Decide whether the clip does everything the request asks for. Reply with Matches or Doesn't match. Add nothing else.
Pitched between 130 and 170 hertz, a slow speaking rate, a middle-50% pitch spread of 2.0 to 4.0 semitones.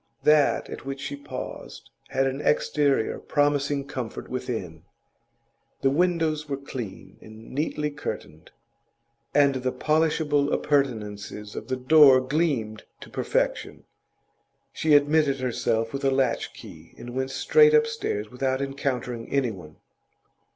Matches